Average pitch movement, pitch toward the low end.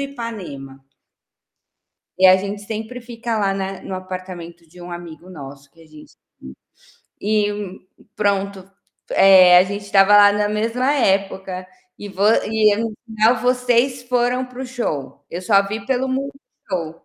No: average, 4.0 semitones; high, 200 Hz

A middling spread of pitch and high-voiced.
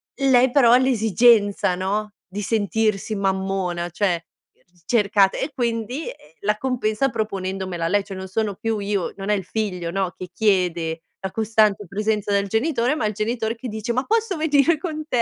Yes: average, 3.5 semitones; high, 210 Hz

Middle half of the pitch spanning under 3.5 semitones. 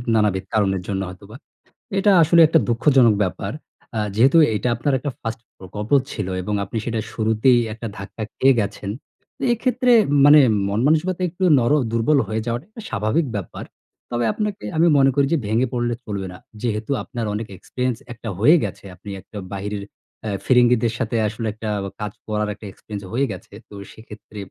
No: average, 4.2 semitones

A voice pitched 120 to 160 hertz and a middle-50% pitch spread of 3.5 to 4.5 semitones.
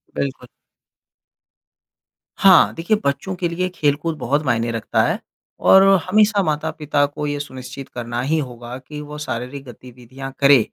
Yes: medium, 140 Hz; average, 3.8 semitones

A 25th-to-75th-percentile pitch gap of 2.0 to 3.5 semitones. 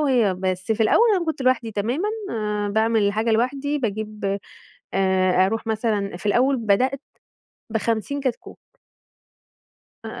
No: average, 4.1 semitones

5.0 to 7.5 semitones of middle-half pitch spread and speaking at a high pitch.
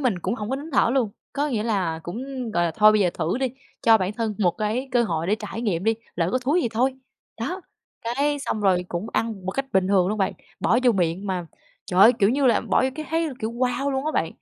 Yes: average, 5.3 semitones; high, 220 Hz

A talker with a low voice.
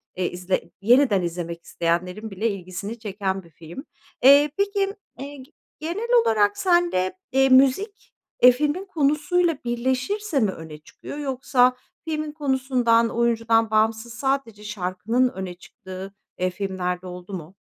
No: high, 230 Hz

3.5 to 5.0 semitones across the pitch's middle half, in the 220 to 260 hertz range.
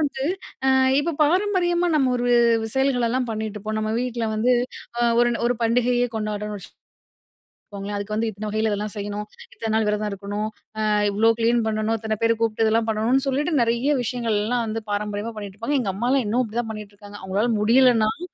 No: average, 2.7 semitones; high, 225 Hz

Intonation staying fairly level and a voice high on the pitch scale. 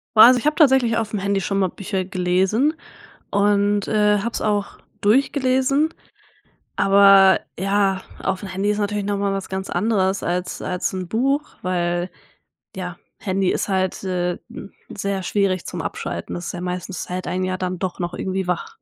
Yes: narrow, 2.0 semitones; high, 195 Hz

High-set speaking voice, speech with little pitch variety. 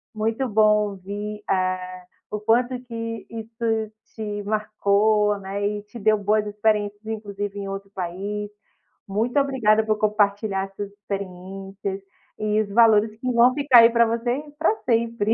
Yes: high, 210 Hz; narrow, 2.1 semitones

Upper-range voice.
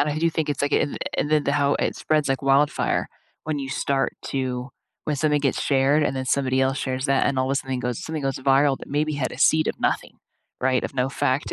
No: medium, 140 Hz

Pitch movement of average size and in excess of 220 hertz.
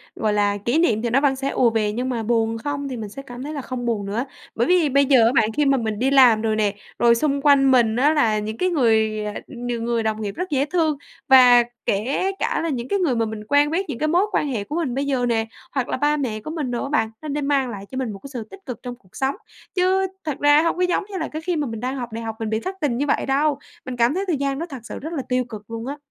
Yes: average, 4.4 semitones; very high, 255 Hz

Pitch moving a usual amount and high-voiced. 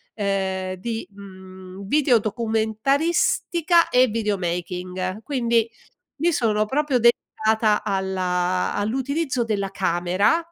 Yes: average, 4.5 semitones; high, 215 Hz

